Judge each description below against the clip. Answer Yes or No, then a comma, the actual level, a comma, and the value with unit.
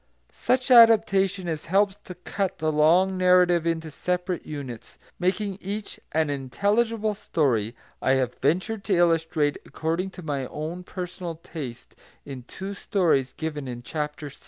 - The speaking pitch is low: No, medium, 170 Hz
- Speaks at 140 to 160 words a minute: Yes, average, 145 wpm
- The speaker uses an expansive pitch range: No, average, 4.5 semitones